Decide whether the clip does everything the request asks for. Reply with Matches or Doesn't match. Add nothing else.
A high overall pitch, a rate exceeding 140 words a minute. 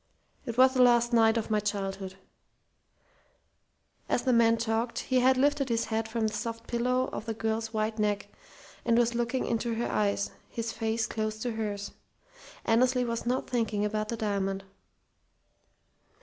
Matches